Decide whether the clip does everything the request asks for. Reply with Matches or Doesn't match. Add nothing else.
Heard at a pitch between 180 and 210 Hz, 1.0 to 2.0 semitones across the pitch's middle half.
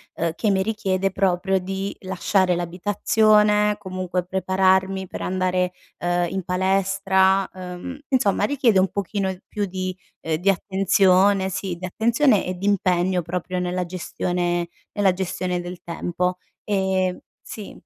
Matches